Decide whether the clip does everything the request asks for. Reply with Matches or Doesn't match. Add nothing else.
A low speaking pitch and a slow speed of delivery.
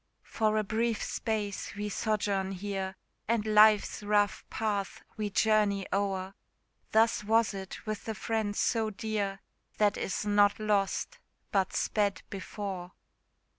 Doesn't match